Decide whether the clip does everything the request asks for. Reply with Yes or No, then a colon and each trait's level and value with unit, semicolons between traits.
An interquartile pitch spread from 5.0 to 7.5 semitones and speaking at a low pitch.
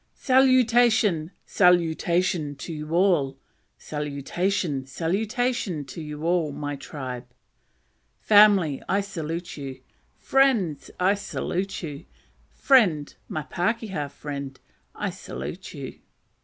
No: wide, 5.5 semitones; medium, 170 Hz